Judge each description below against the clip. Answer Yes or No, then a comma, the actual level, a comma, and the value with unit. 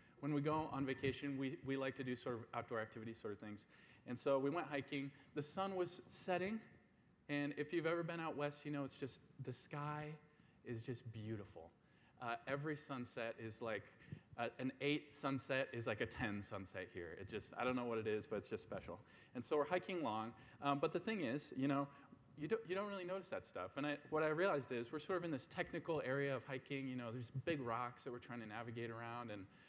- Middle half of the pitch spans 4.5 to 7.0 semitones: No, average, 4.0 semitones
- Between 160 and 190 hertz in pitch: No, low, 135 Hz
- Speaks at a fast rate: Yes, fast, 235 wpm